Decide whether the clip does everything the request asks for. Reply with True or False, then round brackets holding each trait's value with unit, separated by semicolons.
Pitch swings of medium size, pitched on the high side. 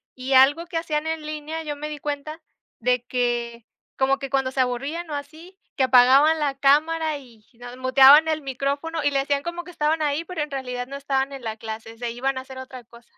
True (3.1 semitones; 275 Hz)